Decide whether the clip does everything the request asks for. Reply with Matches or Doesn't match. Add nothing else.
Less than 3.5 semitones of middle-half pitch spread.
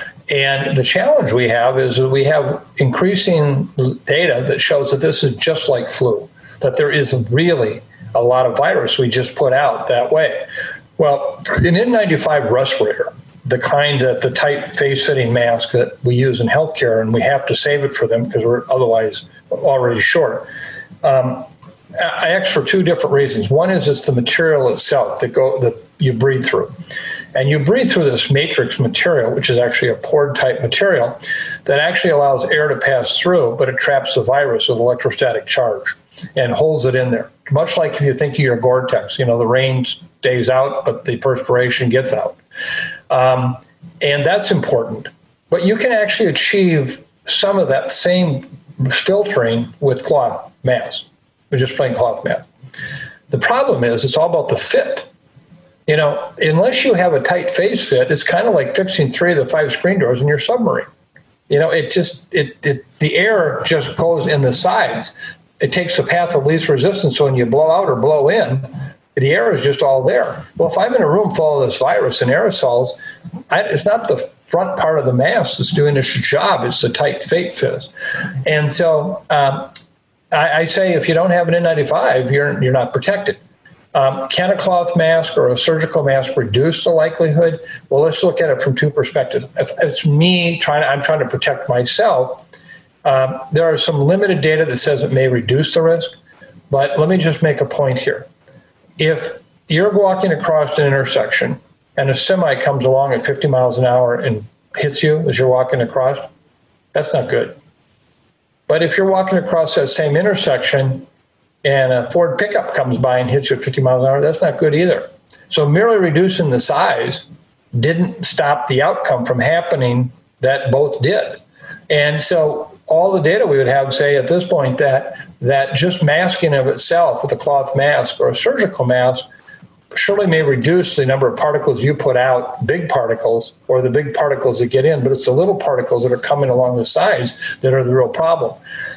Doesn't match